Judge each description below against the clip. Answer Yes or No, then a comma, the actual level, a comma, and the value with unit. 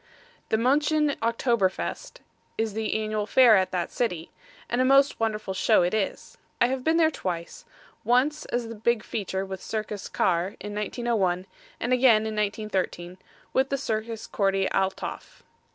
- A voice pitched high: Yes, high, 220 Hz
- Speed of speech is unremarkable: Yes, average, 160 wpm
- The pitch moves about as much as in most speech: Yes, average, 4.0 semitones